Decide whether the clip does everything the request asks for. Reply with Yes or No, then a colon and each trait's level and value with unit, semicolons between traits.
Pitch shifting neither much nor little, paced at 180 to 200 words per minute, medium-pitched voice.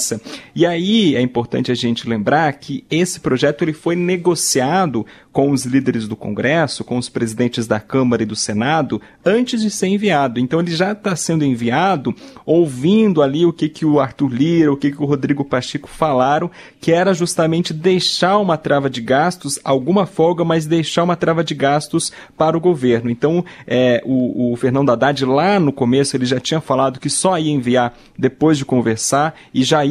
Yes: average, 4.7 semitones; fast, 185 wpm; medium, 145 Hz